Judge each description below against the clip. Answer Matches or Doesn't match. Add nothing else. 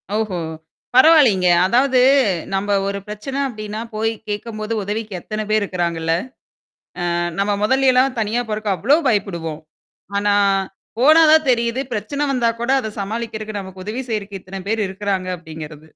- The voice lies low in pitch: Doesn't match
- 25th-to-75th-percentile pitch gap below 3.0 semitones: Doesn't match